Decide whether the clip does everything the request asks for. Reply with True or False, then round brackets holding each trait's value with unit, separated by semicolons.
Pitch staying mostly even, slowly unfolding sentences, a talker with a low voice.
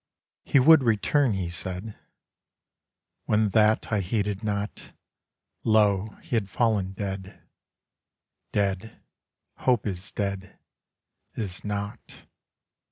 True (2.3 semitones; 100 wpm; 105 Hz)